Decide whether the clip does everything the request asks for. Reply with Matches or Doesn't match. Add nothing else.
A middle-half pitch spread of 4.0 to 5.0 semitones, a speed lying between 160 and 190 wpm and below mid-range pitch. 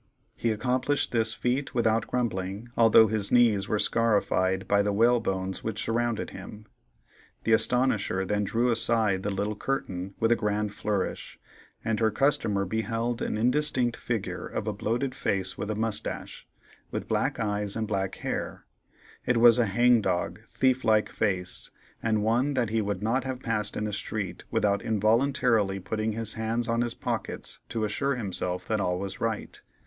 Doesn't match